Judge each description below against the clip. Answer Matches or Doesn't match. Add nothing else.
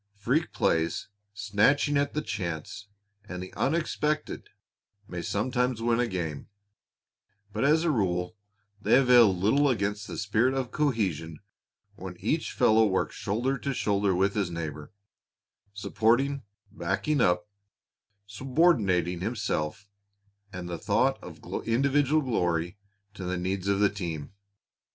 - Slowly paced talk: Matches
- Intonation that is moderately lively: Doesn't match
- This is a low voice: Matches